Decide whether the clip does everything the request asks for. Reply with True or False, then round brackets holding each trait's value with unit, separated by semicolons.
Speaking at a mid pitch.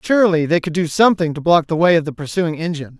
True (165 Hz)